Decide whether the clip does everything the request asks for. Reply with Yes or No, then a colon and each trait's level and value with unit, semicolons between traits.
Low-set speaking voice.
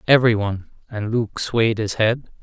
Yes: low, 110 Hz